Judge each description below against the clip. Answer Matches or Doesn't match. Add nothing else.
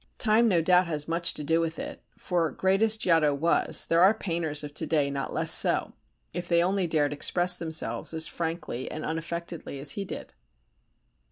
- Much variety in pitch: Doesn't match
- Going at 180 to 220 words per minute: Matches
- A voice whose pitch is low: Doesn't match